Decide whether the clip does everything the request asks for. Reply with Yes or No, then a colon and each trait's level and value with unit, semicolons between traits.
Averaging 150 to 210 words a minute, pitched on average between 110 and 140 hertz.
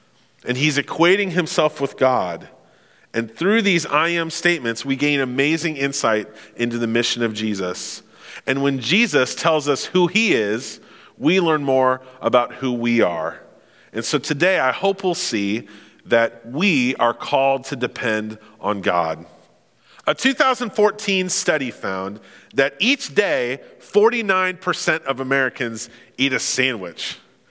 No: average, 140 wpm; low, 135 Hz